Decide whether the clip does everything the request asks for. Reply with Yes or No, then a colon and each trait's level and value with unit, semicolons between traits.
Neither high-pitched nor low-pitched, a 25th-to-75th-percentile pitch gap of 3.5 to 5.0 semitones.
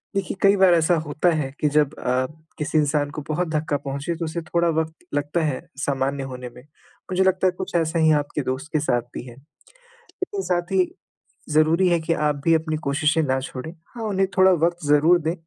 No: medium, 155 Hz; average, 3.1 semitones